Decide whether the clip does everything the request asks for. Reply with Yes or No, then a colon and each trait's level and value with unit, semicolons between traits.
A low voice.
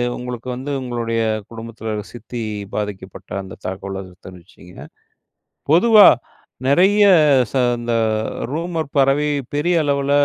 Yes: low, 125 Hz